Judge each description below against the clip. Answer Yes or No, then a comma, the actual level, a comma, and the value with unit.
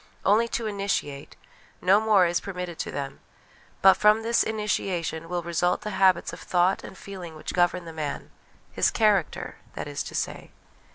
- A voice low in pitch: No, medium, 185 Hz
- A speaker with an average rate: Yes, average, 170 wpm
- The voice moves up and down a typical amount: Yes, average, 3.4 semitones